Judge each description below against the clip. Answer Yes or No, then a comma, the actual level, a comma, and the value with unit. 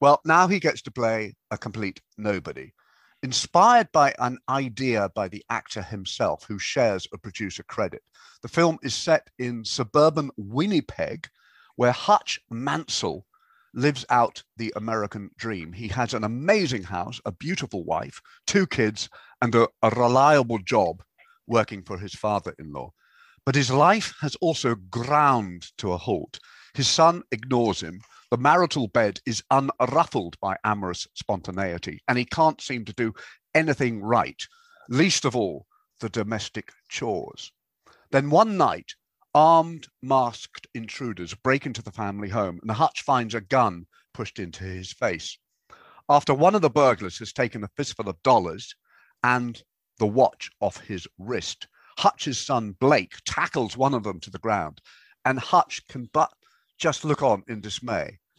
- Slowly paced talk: No, average, 155 wpm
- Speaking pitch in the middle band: No, low, 120 Hz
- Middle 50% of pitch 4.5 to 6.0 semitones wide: Yes, wide, 5.4 semitones